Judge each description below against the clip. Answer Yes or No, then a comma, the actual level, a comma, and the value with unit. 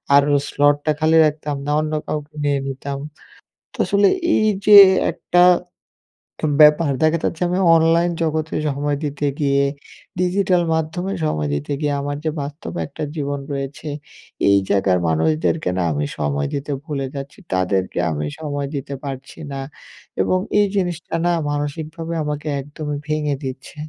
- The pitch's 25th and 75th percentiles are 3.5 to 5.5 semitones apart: No, narrow, 2.4 semitones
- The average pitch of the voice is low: No, medium, 145 Hz